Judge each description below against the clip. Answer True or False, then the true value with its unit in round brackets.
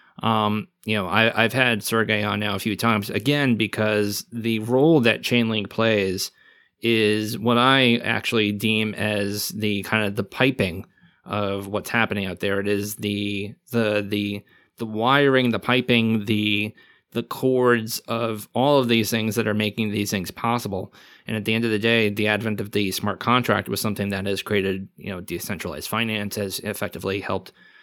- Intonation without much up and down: True (2.0 semitones)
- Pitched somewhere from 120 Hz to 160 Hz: False (105 Hz)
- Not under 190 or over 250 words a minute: False (180 wpm)